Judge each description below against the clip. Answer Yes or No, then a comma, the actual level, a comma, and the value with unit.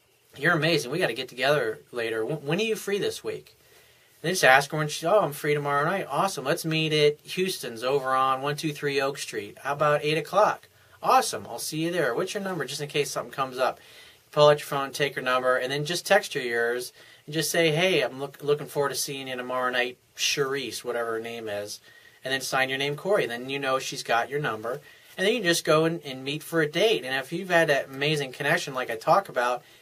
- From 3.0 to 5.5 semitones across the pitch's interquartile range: Yes, average, 3.4 semitones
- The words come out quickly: Yes, fast, 240 wpm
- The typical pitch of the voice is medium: Yes, medium, 145 Hz